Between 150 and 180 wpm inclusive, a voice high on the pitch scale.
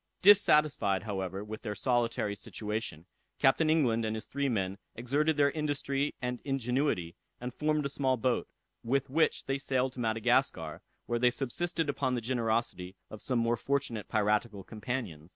No: average, 155 wpm; low, 125 Hz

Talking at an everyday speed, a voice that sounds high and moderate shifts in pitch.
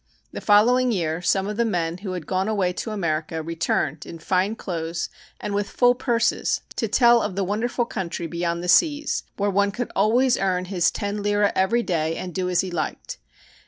Yes: average, 195 wpm; high, 195 Hz; average, 4.0 semitones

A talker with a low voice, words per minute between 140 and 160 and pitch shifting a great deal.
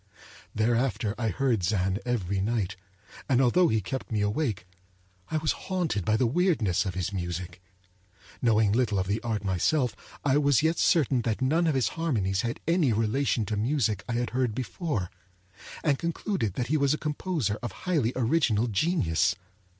No: low, 115 Hz; average, 170 wpm; wide, 5.7 semitones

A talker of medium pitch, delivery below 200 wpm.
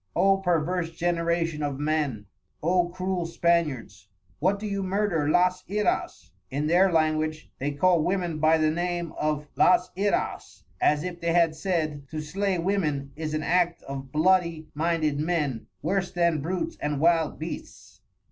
Yes: medium, 165 Hz; average, 155 wpm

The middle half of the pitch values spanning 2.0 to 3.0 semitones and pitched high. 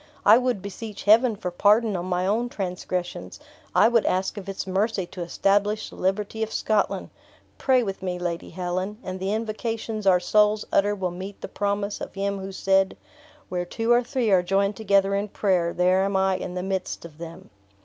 Yes: narrow, 2.5 semitones; high, 195 Hz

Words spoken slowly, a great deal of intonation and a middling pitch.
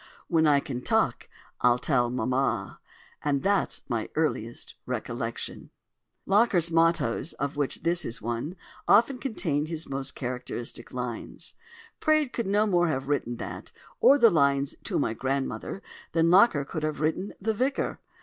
No: average, 150 wpm; wide, 6.4 semitones; medium, 155 Hz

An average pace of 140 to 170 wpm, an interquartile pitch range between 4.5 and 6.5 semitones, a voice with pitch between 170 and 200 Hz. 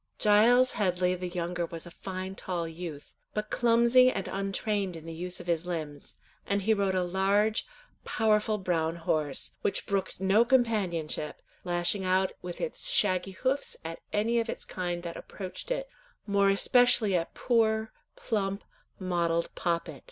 No: average, 155 wpm; average, 3.7 semitones; high, 190 Hz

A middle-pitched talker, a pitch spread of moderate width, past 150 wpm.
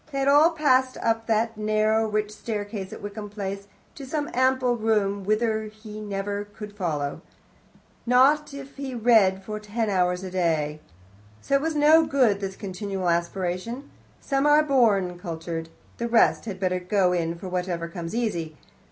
No: high, 210 Hz; average, 4.8 semitones; average, 170 wpm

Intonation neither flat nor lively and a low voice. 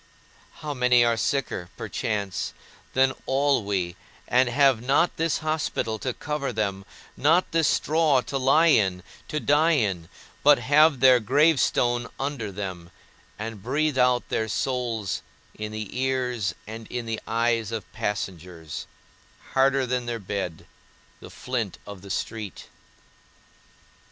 Yes: average, 4.7 semitones; low, 120 Hz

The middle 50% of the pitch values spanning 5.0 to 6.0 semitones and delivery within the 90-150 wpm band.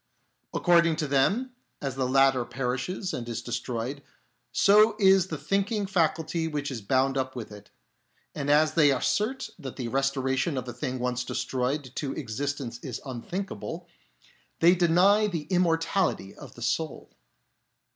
Yes: wide, 5.4 semitones; average, 145 wpm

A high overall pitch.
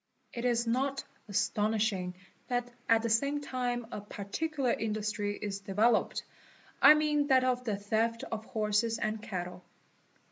Yes: high, 225 Hz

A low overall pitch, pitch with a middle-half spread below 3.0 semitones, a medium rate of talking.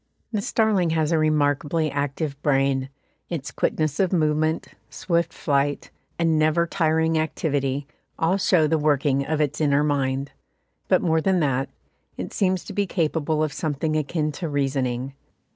No: medium, 155 Hz; narrow, 2.5 semitones; average, 150 wpm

